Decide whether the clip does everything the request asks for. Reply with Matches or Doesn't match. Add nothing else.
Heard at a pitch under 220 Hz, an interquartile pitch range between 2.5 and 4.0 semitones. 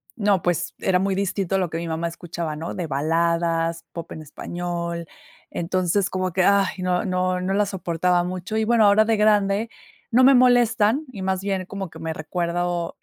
Matches